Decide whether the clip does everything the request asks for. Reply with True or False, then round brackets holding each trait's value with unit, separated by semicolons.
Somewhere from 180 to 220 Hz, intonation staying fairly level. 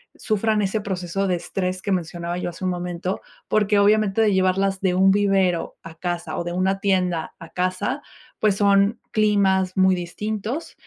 True (190 Hz; 2.1 semitones)